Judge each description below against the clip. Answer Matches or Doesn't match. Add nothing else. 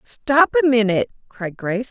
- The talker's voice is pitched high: Matches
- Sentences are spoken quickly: Doesn't match